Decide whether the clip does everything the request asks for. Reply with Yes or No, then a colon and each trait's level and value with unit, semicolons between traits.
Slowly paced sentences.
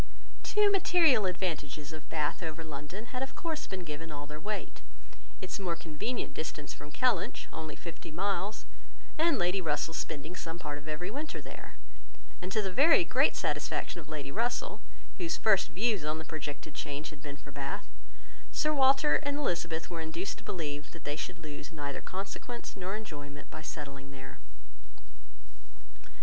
No: average, 165 wpm